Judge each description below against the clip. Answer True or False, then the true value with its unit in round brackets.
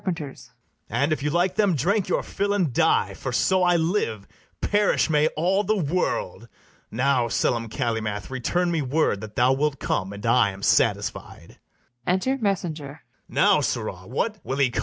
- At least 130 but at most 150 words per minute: False (165 wpm)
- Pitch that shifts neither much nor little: False (7.2 semitones)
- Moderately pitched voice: True (150 Hz)